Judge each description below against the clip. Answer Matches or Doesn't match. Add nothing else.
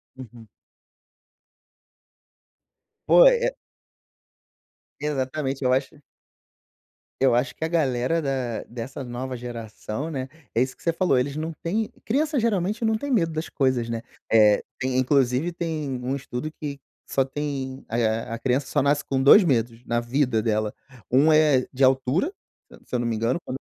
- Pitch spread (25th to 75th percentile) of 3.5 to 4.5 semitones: Matches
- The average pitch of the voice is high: Doesn't match